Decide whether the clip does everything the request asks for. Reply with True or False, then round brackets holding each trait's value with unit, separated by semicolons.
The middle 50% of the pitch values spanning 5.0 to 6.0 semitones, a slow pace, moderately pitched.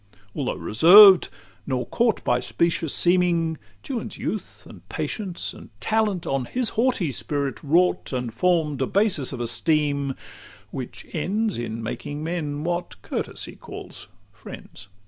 True (5.3 semitones; 130 wpm; 160 Hz)